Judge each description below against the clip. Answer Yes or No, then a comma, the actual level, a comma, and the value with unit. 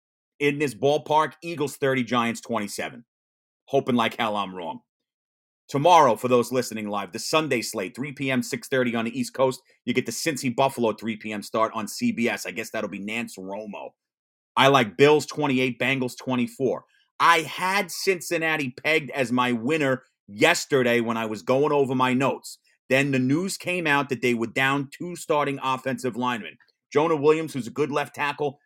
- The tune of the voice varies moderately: Yes, average, 4.0 semitones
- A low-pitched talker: Yes, low, 130 Hz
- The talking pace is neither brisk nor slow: Yes, average, 175 wpm